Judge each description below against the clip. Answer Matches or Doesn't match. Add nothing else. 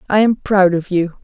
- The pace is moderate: Doesn't match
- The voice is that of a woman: Matches